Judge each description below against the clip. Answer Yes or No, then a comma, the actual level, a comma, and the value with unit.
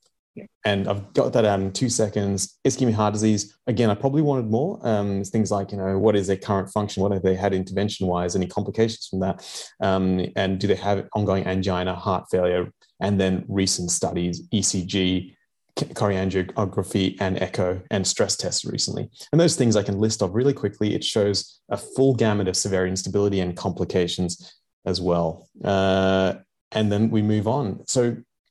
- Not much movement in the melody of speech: Yes, narrow, 2.3 semitones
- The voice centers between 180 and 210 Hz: No, low, 100 Hz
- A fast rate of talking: No, average, 180 wpm